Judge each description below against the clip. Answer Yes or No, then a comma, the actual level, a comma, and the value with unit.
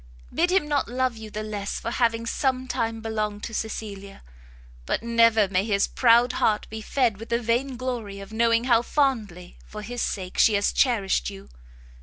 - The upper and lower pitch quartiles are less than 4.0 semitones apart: Yes, average, 2.8 semitones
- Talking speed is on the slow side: No, average, 185 wpm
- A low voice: No, high, 225 Hz